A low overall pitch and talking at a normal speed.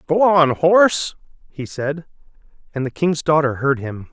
No: medium, 155 Hz; average, 160 wpm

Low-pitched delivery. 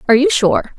No: very high, 265 Hz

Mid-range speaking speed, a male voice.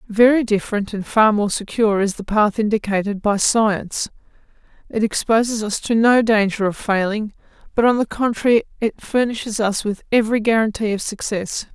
No: average, 165 wpm; female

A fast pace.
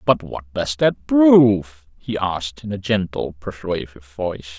No: average, 155 wpm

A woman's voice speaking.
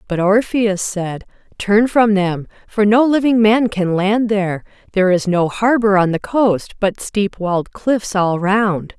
Yes: female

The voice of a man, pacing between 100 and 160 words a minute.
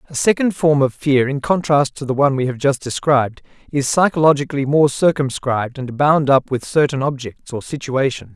No: male; average, 185 wpm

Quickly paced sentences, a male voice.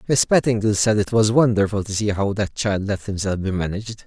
Yes: fast, 220 wpm; male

